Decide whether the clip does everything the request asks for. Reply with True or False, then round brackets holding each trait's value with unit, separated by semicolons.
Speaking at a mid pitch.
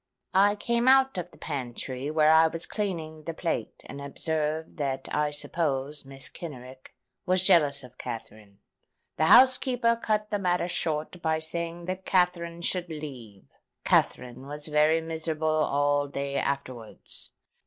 True (155 Hz)